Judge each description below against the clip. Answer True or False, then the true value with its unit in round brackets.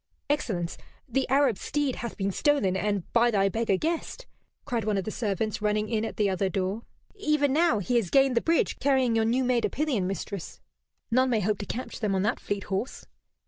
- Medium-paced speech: False (210 wpm)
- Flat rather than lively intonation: False (4.8 semitones)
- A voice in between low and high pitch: False (225 Hz)